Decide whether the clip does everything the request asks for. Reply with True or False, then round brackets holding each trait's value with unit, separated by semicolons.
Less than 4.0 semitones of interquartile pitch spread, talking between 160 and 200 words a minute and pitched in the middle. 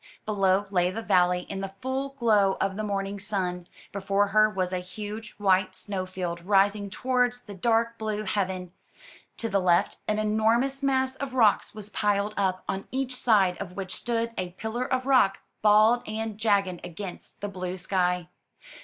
False (3.0 semitones; 170 wpm; 205 Hz)